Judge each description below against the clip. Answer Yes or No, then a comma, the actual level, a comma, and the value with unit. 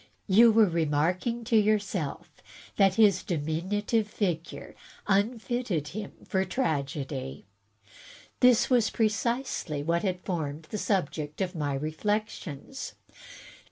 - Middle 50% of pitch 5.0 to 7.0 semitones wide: Yes, wide, 5.6 semitones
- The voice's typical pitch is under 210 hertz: Yes, high, 190 Hz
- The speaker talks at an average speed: No, slow, 110 wpm